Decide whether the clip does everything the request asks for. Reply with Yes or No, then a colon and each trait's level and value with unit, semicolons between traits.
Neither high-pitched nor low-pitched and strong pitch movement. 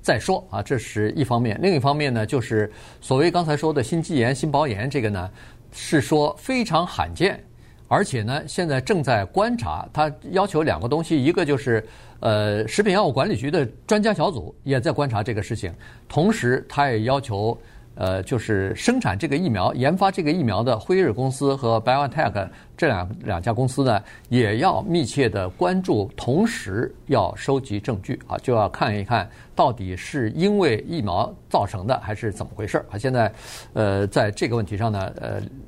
No: low, 125 Hz; wide, 6.0 semitones